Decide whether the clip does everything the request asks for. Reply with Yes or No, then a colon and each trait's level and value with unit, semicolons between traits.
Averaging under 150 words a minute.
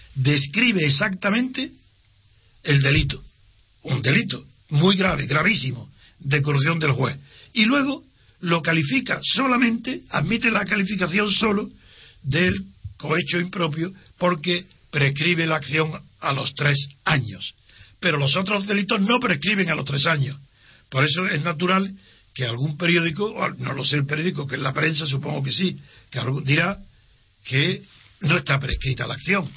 Yes: average, 140 wpm